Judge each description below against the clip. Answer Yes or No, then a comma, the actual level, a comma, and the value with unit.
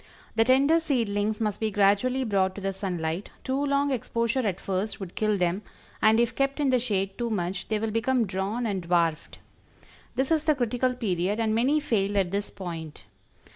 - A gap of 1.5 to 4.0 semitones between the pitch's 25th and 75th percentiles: No, average, 4.6 semitones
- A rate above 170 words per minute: Yes, average, 190 wpm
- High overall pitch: Yes, high, 215 Hz